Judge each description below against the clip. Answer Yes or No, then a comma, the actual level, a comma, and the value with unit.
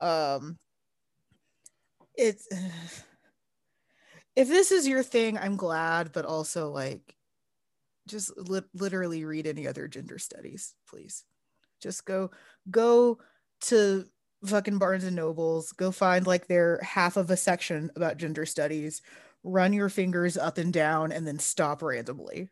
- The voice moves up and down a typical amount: Yes, average, 3.4 semitones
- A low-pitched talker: No, medium, 180 Hz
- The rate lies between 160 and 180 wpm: No, slow, 135 wpm